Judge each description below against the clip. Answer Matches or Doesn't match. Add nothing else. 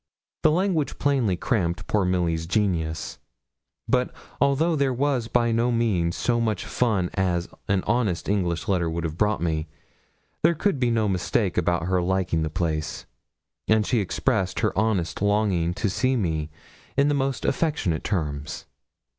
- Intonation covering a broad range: Matches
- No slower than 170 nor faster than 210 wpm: Doesn't match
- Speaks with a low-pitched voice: Matches